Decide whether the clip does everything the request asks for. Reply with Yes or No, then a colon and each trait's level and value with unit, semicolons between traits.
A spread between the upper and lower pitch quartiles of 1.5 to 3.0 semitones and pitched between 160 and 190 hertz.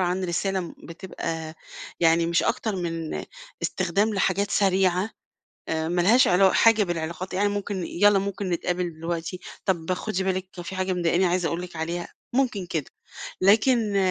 Yes: narrow, 2.5 semitones; medium, 185 Hz